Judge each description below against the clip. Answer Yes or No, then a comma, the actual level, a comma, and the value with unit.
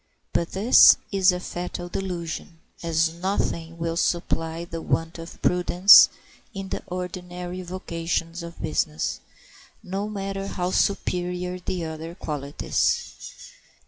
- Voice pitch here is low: No, medium, 175 Hz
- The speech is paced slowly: Yes, slow, 115 wpm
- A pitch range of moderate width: No, narrow, 1.9 semitones